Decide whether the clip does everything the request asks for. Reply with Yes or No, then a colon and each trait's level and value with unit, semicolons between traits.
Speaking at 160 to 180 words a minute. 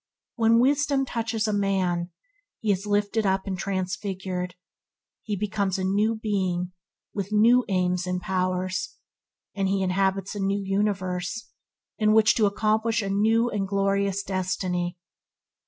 No: average, 140 wpm